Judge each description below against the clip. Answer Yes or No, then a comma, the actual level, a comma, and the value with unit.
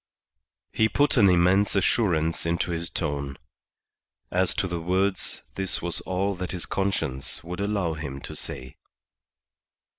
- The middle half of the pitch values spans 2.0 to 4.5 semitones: Yes, average, 3.0 semitones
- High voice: No, very low, 90 Hz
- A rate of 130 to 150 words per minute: Yes, average, 140 wpm